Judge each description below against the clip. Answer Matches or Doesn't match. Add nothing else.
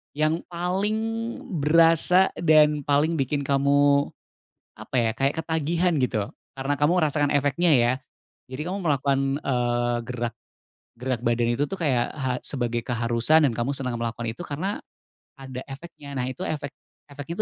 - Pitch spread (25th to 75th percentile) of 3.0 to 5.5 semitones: Matches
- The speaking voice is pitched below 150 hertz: Matches